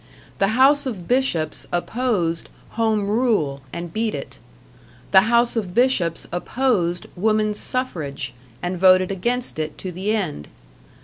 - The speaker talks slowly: Yes, slow, 130 wpm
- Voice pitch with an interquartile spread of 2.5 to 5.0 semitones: No, wide, 5.4 semitones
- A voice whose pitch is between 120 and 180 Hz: No, high, 200 Hz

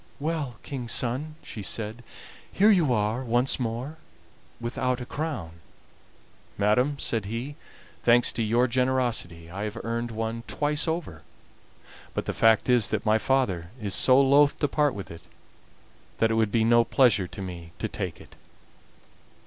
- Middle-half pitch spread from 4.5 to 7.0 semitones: No, average, 3.7 semitones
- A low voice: Yes, low, 120 Hz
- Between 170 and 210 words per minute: No, average, 155 wpm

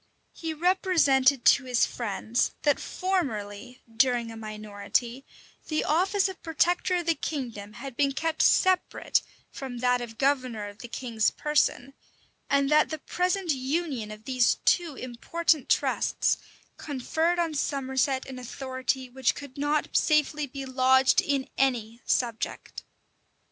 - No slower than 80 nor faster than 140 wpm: Yes, slow, 135 wpm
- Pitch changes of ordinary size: Yes, average, 4.2 semitones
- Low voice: No, very high, 265 Hz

